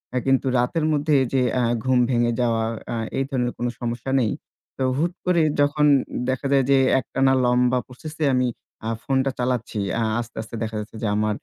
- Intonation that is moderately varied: No, narrow, 2.3 semitones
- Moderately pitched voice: No, low, 125 Hz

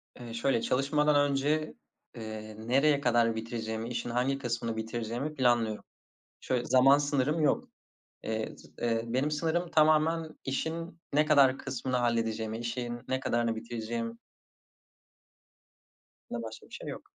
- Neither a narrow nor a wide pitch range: Yes, average, 3.7 semitones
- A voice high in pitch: No, low, 120 Hz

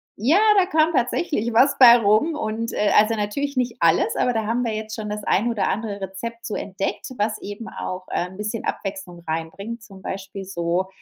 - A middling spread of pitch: Yes, average, 3.4 semitones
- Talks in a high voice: Yes, high, 215 Hz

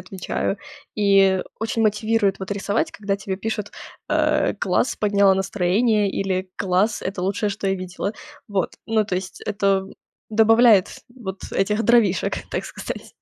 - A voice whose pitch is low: No, high, 200 Hz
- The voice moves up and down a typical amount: No, narrow, 2.0 semitones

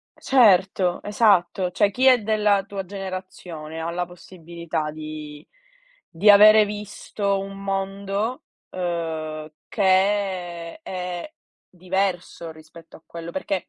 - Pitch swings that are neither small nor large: Yes, average, 3.0 semitones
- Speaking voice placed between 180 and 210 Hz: Yes, medium, 185 Hz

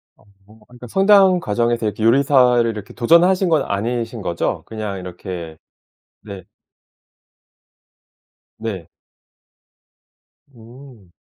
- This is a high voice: No, low, 115 Hz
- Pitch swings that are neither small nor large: Yes, average, 5.0 semitones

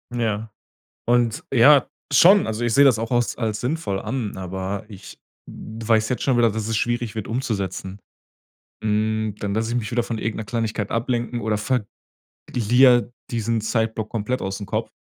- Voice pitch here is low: Yes, low, 115 Hz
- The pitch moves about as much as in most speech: No, narrow, 2.1 semitones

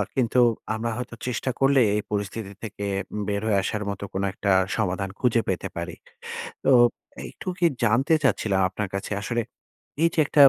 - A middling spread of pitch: Yes, average, 3.6 semitones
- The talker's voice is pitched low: Yes, low, 110 Hz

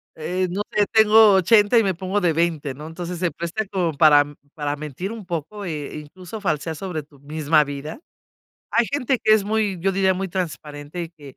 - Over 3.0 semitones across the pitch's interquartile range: Yes, average, 4.5 semitones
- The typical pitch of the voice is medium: Yes, medium, 175 Hz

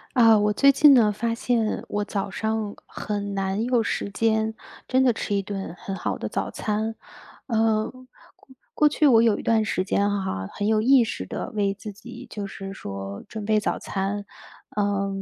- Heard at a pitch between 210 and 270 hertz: Yes, high, 215 Hz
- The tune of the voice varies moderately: No, narrow, 2.2 semitones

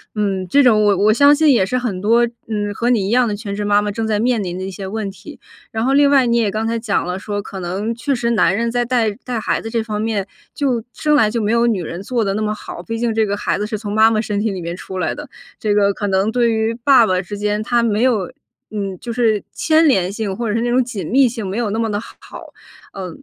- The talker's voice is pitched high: Yes, high, 220 Hz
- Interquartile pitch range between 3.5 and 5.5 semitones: No, average, 2.7 semitones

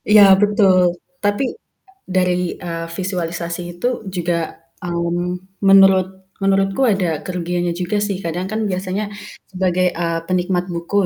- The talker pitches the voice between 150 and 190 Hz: Yes, medium, 185 Hz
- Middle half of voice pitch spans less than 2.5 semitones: Yes, narrow, 1.8 semitones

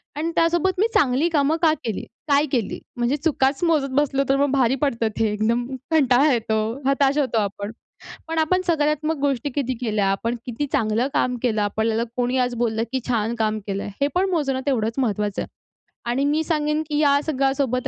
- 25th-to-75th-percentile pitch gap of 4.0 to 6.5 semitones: Yes, average, 4.3 semitones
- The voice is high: Yes, very high, 270 Hz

